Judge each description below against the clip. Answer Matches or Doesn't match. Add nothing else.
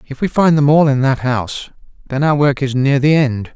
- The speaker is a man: Matches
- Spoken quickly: Matches